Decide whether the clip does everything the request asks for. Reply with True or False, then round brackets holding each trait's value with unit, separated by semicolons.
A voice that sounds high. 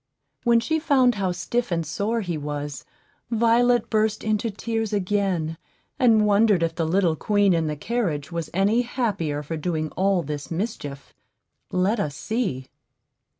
True (195 Hz)